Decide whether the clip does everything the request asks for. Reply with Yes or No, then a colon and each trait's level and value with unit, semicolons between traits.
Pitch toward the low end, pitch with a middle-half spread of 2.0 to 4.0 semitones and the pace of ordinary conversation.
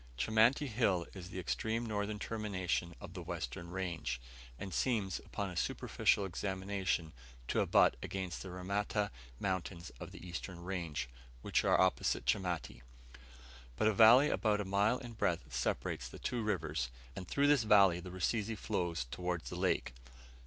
Yes: very low, 95 Hz; average, 3.5 semitones; average, 155 wpm